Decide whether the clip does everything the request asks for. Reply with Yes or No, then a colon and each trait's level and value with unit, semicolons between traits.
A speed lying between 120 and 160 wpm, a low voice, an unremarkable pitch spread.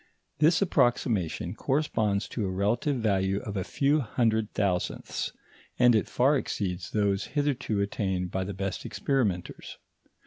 Yes: slow, 135 wpm; low, 105 Hz; average, 4.5 semitones